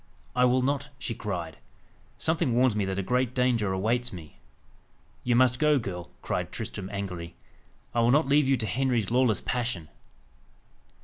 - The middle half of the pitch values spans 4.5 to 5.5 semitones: Yes, average, 4.9 semitones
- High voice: No, low, 120 Hz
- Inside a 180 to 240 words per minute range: No, average, 165 wpm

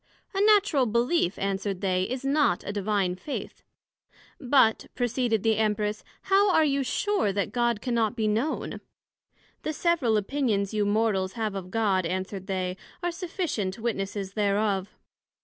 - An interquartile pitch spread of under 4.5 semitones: No, average, 5.2 semitones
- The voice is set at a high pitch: Yes, high, 220 Hz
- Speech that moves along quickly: No, average, 145 wpm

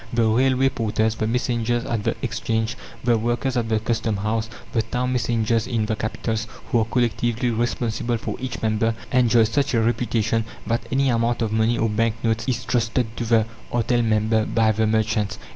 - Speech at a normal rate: Yes, average, 185 wpm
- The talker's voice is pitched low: Yes, low, 115 Hz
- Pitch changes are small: Yes, narrow, 1.4 semitones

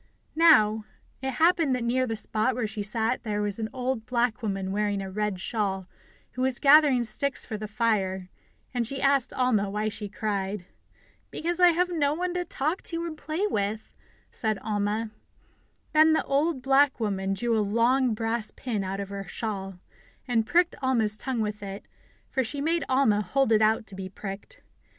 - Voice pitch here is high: Yes, high, 225 Hz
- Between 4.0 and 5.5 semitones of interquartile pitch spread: Yes, average, 4.6 semitones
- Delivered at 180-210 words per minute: Yes, average, 185 wpm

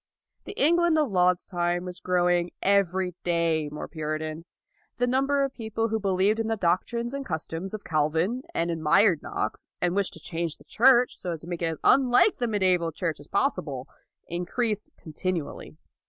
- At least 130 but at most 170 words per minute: No, average, 180 wpm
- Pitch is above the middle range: No, medium, 180 Hz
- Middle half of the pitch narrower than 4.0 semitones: No, average, 5.2 semitones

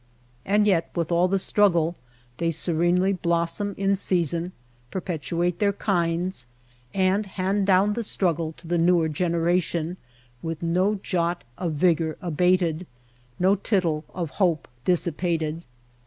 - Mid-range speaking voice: Yes, medium, 175 Hz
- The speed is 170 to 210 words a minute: No, slow, 135 wpm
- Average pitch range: No, narrow, 2.2 semitones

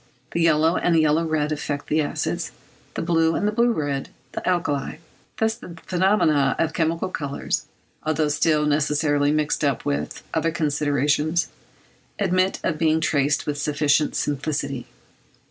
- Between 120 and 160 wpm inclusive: Yes, average, 140 wpm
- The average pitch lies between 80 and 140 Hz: No, medium, 155 Hz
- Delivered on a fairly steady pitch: Yes, narrow, 2.2 semitones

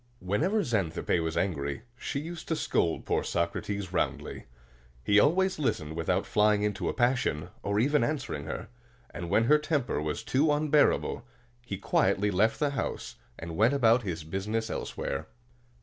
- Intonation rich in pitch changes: Yes, wide, 8.1 semitones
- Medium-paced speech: Yes, average, 155 wpm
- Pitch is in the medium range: No, low, 105 Hz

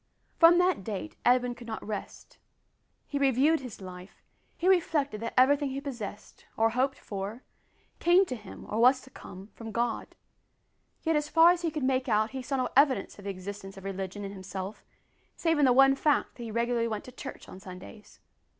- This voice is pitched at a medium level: No, high, 245 Hz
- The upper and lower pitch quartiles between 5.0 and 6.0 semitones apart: Yes, wide, 5.4 semitones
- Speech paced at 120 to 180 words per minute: No, average, 195 wpm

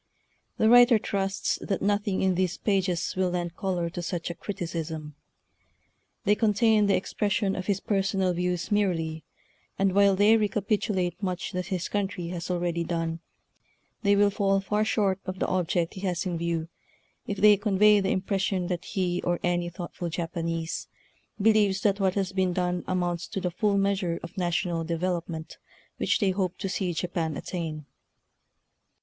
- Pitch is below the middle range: No, medium, 185 Hz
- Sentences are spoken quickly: No, average, 170 wpm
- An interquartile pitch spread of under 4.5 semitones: Yes, narrow, 2.4 semitones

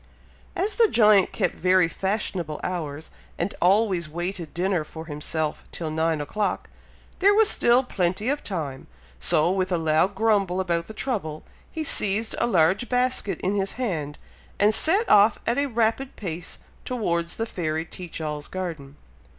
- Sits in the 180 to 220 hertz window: Yes, medium, 185 Hz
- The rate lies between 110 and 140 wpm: No, average, 160 wpm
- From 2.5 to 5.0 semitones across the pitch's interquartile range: No, wide, 5.4 semitones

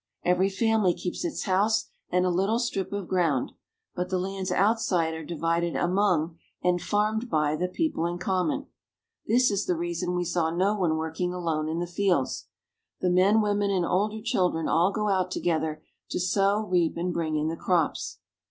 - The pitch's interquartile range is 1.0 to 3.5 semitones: Yes, average, 3.1 semitones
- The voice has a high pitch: No, medium, 180 Hz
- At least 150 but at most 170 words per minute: No, average, 180 wpm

